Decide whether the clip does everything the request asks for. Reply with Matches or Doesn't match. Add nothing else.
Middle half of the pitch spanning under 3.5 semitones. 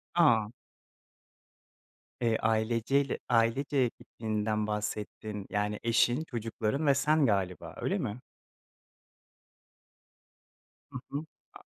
Doesn't match